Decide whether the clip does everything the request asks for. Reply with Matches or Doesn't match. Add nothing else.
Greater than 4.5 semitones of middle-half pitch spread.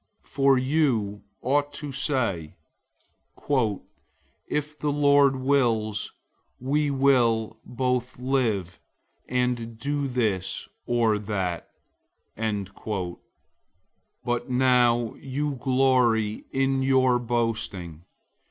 Doesn't match